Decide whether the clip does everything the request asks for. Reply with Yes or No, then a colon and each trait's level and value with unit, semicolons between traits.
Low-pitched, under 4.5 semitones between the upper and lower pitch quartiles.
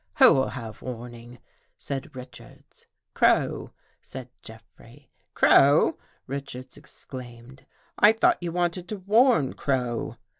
No: low, 130 Hz; average, 4.8 semitones